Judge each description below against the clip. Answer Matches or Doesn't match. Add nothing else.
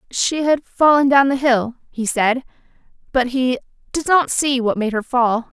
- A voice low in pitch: Doesn't match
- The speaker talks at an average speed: Matches